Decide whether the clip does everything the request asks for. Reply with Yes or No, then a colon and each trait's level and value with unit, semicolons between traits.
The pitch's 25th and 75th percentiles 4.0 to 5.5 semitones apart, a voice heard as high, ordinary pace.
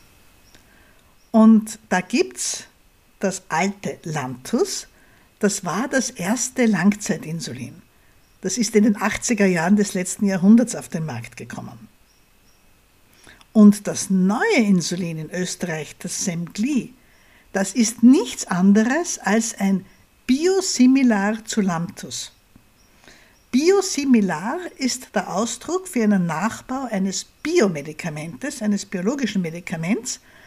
No: average, 4.5 semitones; high, 205 Hz; slow, 105 wpm